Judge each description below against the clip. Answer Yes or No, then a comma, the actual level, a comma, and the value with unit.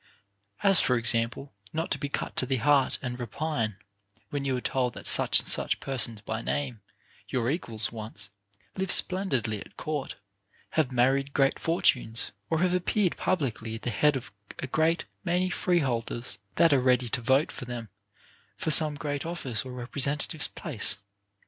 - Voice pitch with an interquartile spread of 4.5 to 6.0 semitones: Yes, average, 4.8 semitones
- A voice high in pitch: No, low, 135 Hz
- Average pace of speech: Yes, average, 170 wpm